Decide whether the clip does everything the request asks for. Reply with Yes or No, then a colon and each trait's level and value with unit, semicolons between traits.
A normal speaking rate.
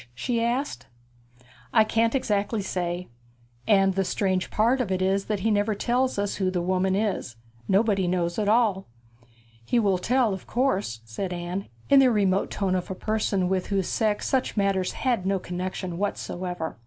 Yes: average, 175 wpm